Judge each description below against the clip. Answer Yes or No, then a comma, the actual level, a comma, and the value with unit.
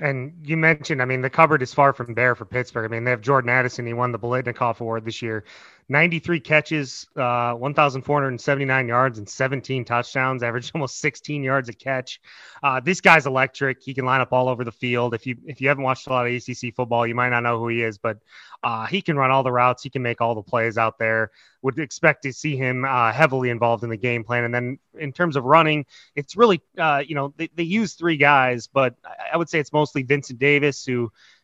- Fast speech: Yes, fast, 235 wpm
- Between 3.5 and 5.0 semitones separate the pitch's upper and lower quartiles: No, average, 3.1 semitones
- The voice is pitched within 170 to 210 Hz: No, low, 130 Hz